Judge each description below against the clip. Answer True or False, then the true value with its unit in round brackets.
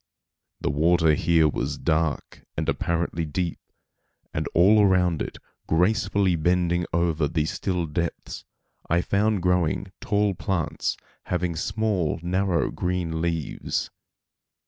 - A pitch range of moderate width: False (2.1 semitones)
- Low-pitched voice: True (85 Hz)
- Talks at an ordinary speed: False (115 wpm)